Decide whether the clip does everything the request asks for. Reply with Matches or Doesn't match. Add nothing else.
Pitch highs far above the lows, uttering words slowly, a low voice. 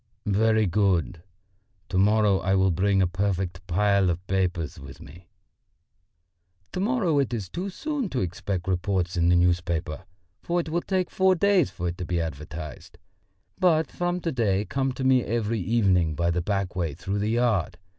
Doesn't match